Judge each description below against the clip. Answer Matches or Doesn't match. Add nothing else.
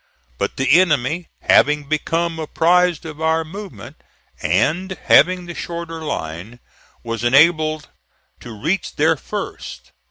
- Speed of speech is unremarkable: Doesn't match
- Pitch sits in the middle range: Matches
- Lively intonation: Doesn't match